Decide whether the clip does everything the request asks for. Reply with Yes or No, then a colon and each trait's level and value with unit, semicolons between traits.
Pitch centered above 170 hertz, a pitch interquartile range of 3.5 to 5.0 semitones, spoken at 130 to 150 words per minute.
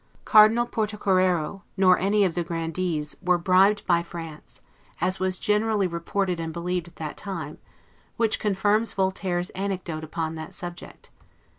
No: medium, 185 Hz; average, 3.0 semitones; average, 140 wpm